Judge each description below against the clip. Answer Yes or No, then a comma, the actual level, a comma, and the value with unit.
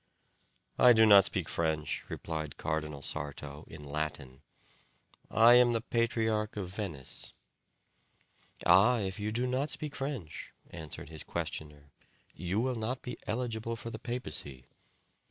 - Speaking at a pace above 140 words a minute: No, slow, 135 wpm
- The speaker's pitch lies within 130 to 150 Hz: No, low, 105 Hz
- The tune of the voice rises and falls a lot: Yes, wide, 7.3 semitones